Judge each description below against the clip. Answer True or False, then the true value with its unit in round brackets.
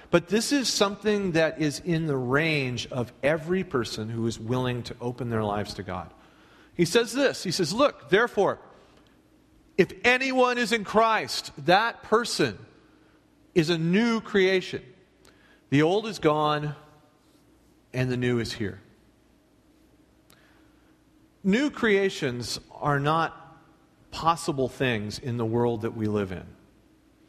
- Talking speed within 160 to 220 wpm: False (135 wpm)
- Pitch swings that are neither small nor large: False (7.9 semitones)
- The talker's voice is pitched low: False (150 Hz)